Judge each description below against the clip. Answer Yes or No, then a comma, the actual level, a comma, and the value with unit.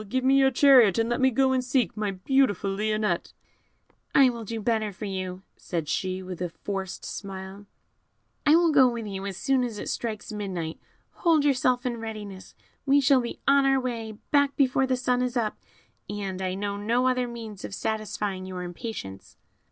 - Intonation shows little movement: No, average, 4.7 semitones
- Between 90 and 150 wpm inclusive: No, average, 190 wpm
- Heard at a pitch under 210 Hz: No, high, 225 Hz